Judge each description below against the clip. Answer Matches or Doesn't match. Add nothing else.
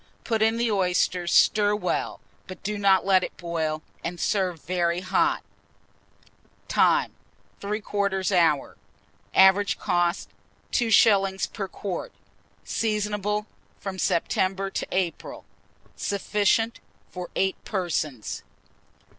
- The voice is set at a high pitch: Matches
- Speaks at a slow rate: Matches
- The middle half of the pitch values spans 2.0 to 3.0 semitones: Matches